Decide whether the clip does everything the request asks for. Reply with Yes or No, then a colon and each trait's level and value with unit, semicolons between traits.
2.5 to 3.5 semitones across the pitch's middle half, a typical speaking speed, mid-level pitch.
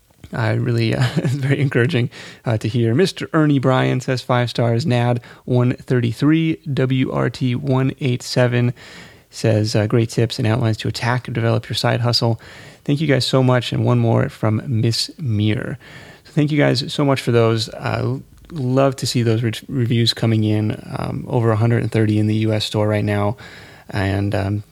No: average, 2.8 semitones; average, 175 wpm; low, 120 Hz